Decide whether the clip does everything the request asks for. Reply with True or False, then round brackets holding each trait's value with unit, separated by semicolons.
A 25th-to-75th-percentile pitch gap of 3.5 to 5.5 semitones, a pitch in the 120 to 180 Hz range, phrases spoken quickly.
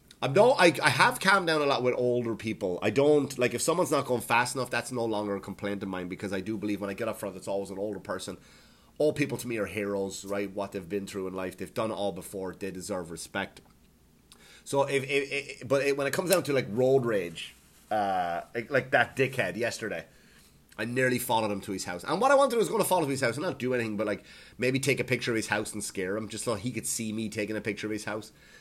False (4.7 semitones; 110 Hz; 275 wpm)